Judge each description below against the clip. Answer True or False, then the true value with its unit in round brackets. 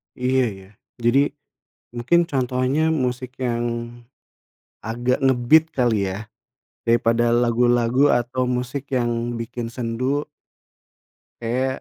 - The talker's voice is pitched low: True (120 Hz)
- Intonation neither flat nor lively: False (1.7 semitones)